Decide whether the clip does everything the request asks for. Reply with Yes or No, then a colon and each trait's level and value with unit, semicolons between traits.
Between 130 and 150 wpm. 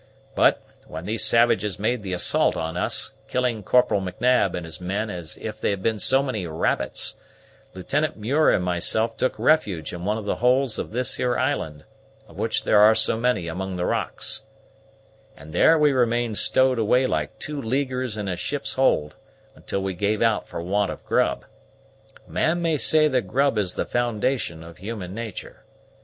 No: average, 185 wpm